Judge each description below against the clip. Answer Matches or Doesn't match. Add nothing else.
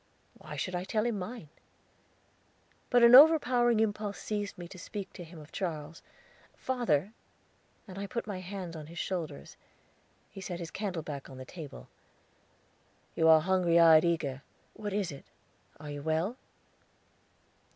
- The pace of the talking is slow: Doesn't match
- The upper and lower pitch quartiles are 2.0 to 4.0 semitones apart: Doesn't match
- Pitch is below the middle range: Doesn't match